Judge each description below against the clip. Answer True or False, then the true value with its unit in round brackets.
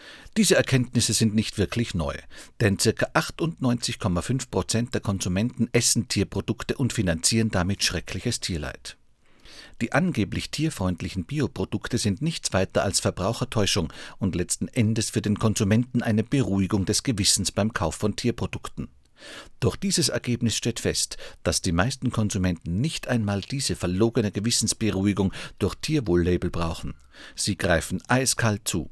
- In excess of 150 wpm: False (130 wpm)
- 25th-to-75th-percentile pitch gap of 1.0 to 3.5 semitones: False (4.3 semitones)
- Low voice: True (110 Hz)